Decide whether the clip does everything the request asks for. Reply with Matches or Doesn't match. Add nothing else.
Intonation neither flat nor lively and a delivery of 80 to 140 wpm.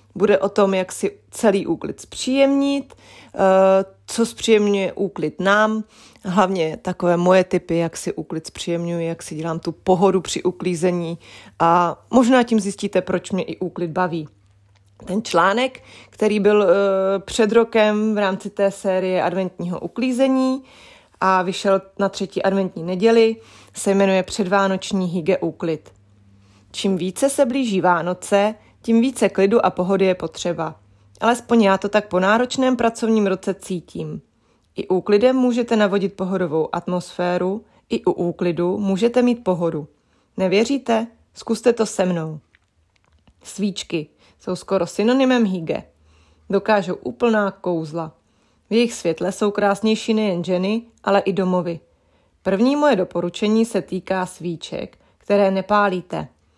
Matches